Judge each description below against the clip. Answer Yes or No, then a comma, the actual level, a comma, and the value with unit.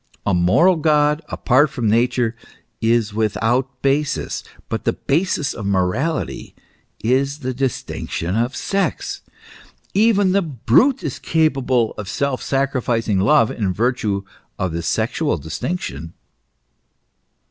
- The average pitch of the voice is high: No, low, 125 Hz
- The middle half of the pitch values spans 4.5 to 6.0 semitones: Yes, wide, 5.6 semitones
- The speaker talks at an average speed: No, slow, 115 wpm